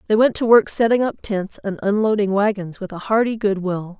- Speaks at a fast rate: Yes, fast, 225 wpm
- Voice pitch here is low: No, high, 205 Hz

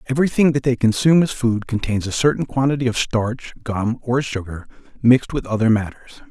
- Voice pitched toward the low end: Yes, low, 120 Hz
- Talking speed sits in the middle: Yes, average, 180 wpm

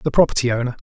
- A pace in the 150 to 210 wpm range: Yes, fast, 205 wpm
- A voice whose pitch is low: Yes, low, 130 Hz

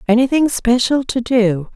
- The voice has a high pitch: Yes, high, 240 Hz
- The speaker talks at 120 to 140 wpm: Yes, slow, 135 wpm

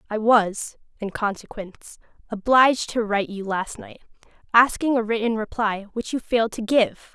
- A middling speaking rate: Yes, average, 160 wpm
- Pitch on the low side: No, high, 220 Hz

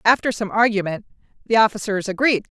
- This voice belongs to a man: No, female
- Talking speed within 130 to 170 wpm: Yes, average, 140 wpm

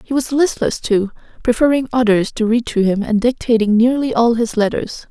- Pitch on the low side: No, high, 235 Hz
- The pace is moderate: Yes, average, 190 wpm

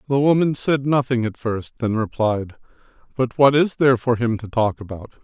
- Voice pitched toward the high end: No, low, 120 Hz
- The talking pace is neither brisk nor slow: Yes, average, 195 wpm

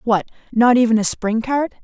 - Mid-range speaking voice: No, high, 235 Hz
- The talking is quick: No, average, 195 wpm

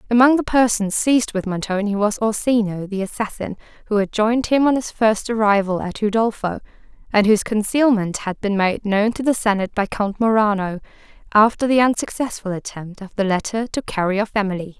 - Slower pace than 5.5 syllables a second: No, 5.6 syllables/s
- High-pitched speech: Yes, high, 210 Hz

